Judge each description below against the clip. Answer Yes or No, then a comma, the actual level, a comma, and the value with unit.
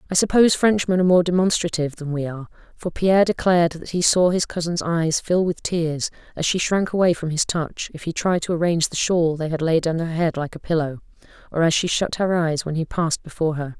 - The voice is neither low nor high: Yes, medium, 170 Hz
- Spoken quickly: Yes, fast, 240 wpm